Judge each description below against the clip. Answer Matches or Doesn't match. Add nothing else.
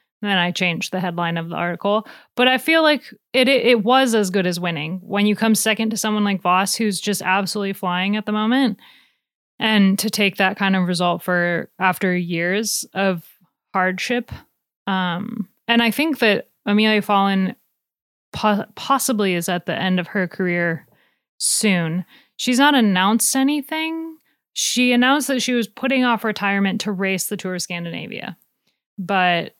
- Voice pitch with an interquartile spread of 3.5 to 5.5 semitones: Matches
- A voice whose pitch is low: Doesn't match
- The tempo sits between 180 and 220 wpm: Doesn't match